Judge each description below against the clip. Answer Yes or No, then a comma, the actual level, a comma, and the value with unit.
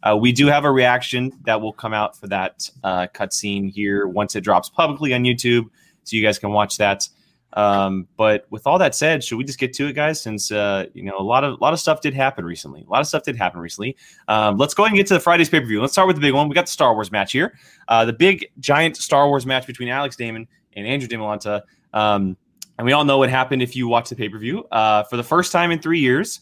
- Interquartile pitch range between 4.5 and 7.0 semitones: Yes, wide, 5.4 semitones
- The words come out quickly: Yes, fast, 275 wpm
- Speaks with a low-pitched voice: Yes, low, 120 Hz